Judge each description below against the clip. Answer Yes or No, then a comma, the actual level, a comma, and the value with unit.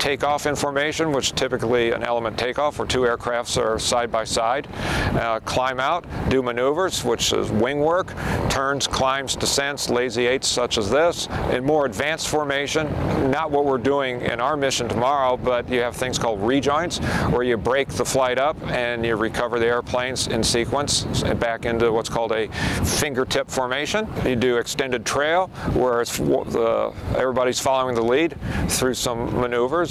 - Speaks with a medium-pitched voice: No, low, 125 Hz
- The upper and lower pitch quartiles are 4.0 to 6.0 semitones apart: No, average, 2.7 semitones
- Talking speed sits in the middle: Yes, average, 170 wpm